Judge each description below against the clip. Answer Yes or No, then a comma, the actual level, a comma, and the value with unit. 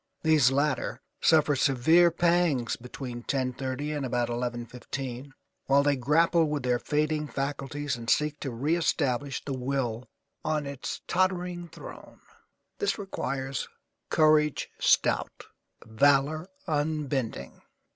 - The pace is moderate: No, slow, 110 wpm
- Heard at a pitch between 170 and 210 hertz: No, medium, 140 Hz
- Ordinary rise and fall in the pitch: Yes, average, 3.3 semitones